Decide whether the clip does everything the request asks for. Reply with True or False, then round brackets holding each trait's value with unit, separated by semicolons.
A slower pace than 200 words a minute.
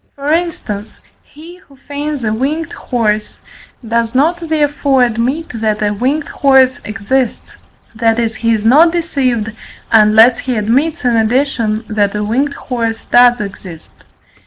True (140 wpm)